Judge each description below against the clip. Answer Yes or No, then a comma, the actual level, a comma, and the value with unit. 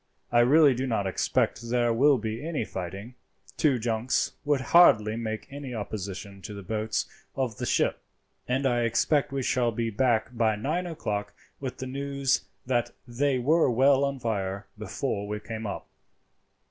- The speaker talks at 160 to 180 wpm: Yes, average, 165 wpm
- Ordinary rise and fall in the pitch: Yes, average, 3.9 semitones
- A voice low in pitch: Yes, low, 120 Hz